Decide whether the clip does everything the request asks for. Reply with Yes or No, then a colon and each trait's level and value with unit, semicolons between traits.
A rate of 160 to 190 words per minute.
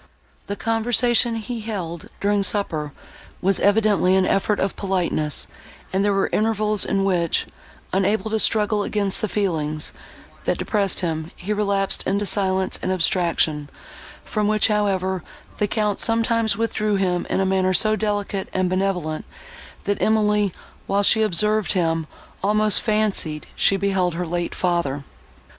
No: average, 145 wpm